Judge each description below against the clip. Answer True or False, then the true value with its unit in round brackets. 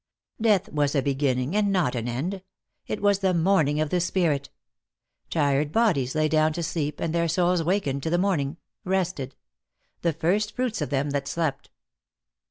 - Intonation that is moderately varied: True (4.7 semitones)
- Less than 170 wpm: False (175 wpm)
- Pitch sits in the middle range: True (160 Hz)